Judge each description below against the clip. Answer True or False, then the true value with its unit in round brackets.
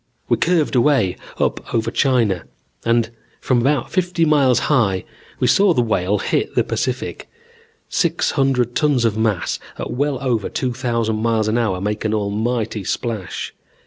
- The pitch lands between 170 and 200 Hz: False (115 Hz)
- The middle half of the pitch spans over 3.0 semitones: True (3.7 semitones)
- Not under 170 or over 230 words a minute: False (155 wpm)